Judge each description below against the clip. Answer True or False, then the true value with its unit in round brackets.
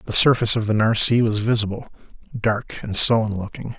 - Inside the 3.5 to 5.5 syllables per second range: False (5.9 syllables/s)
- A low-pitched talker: True (110 Hz)